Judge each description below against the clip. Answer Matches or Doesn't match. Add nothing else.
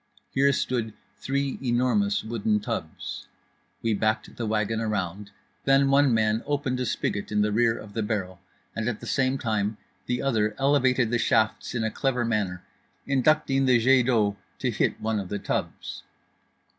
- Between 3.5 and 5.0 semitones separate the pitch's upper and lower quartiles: Matches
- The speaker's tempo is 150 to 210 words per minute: Matches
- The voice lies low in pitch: Matches